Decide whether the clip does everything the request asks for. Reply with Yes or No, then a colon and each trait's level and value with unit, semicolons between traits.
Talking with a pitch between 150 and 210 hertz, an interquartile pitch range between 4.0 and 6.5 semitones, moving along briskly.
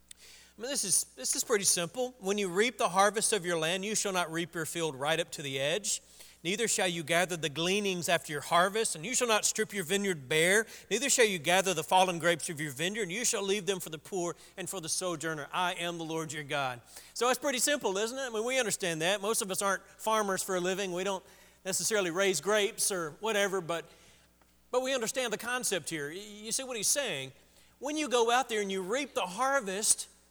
Yes: high, 190 Hz; average, 4.5 semitones; fast, 240 wpm